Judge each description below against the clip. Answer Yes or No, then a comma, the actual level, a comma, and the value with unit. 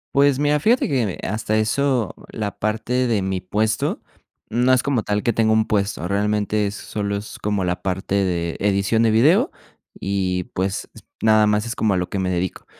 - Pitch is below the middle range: Yes, low, 105 Hz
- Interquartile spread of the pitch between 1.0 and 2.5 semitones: No, average, 2.9 semitones